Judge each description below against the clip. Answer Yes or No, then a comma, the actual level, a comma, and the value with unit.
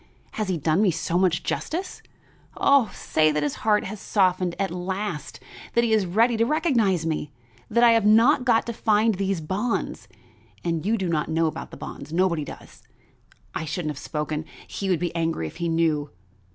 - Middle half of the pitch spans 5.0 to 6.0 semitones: Yes, average, 5.3 semitones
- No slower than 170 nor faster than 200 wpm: Yes, average, 190 wpm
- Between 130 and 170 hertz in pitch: No, medium, 185 Hz